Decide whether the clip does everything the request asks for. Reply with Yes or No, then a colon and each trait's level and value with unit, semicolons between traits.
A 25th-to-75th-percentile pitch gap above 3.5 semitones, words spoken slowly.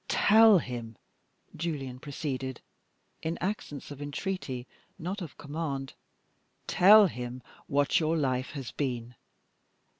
Yes: average, 4.6 semitones; slow, 110 wpm